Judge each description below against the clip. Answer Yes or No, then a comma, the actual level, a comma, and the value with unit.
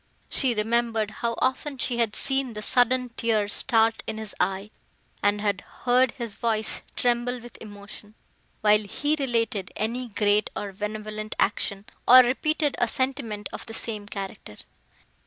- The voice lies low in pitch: No, high, 225 Hz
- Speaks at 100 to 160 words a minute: Yes, average, 150 wpm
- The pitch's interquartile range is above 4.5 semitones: No, average, 2.8 semitones